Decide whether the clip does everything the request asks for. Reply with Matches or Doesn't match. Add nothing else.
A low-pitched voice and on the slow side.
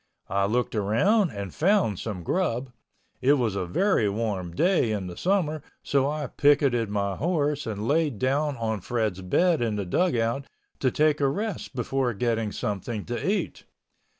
Doesn't match